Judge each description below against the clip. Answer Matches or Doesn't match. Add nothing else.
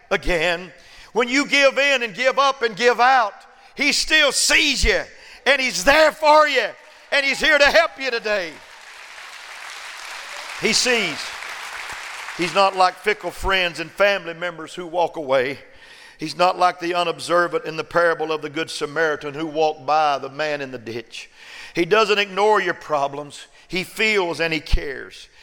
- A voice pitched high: Doesn't match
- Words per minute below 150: Doesn't match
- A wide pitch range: Matches